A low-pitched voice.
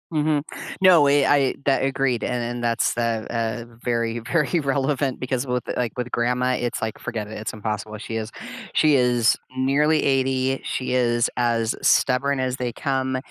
Yes: low, 125 Hz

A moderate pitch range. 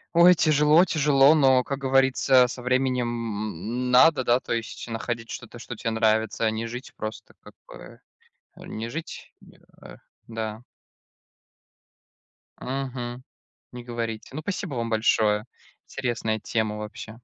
Yes: average, 3.1 semitones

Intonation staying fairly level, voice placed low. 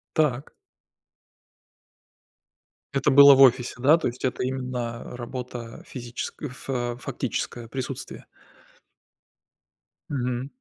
Yes: narrow, 1.7 semitones; low, 125 Hz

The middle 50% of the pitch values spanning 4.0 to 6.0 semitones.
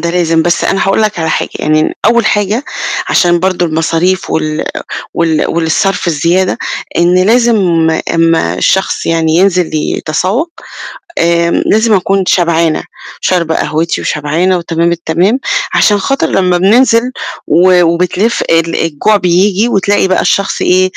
No: average, 2.9 semitones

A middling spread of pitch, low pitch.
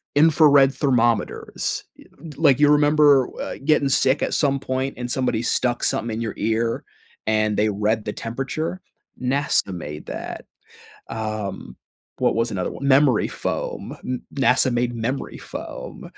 Yes: average, 3.9 semitones; low, 125 Hz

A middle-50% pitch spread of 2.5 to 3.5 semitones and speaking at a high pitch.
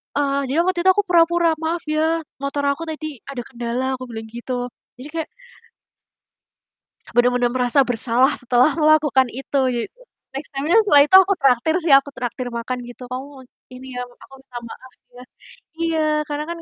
No: average, 3.9 semitones; very high, 270 Hz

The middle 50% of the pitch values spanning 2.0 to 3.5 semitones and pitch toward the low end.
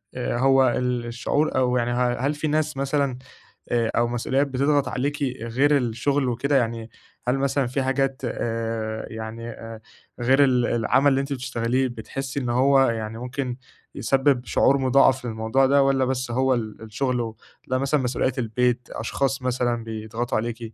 Yes: narrow, 2.5 semitones; low, 125 Hz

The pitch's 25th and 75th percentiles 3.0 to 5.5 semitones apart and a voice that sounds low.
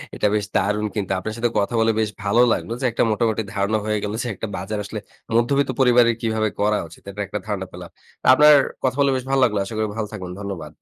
No: narrow, 2.6 semitones; low, 110 Hz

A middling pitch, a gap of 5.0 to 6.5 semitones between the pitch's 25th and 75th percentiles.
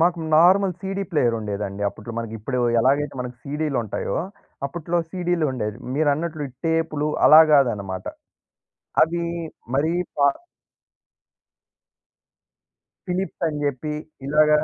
Yes: medium, 150 Hz; average, 5.3 semitones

